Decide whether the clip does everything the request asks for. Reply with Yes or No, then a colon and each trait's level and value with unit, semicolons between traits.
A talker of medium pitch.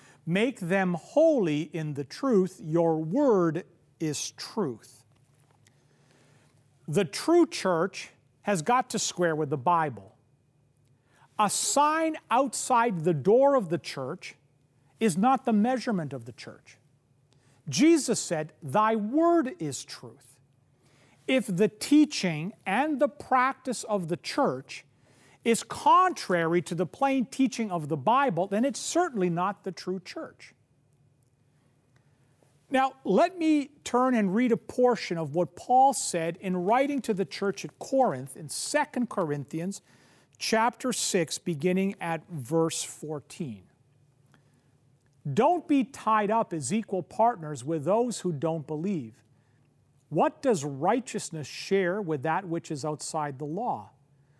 Yes: medium, 170 Hz